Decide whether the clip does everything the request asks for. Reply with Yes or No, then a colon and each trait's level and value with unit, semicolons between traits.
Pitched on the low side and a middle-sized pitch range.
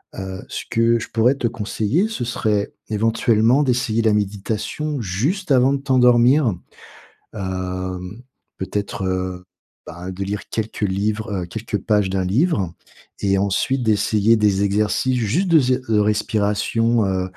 Yes: low, 105 Hz; average, 3.7 semitones